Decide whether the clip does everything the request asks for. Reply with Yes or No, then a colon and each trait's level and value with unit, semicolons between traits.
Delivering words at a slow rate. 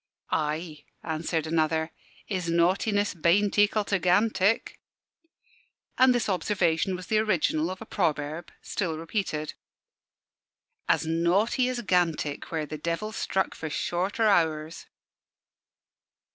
Yes: slow, 115 wpm